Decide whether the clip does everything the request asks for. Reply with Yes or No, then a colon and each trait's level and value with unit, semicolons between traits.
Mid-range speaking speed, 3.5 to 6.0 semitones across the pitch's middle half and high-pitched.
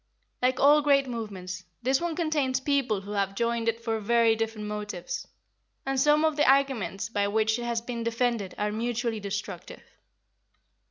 Yes: average, 165 wpm; average, 4.1 semitones; high, 230 Hz